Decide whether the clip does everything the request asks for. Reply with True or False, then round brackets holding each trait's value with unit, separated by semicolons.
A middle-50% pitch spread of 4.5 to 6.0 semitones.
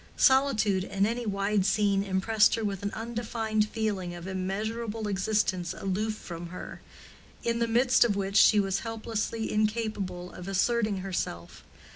False (2.7 semitones)